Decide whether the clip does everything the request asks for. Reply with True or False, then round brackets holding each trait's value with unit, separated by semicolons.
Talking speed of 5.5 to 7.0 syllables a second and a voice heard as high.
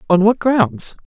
False (3.8 syllables/s; 200 Hz)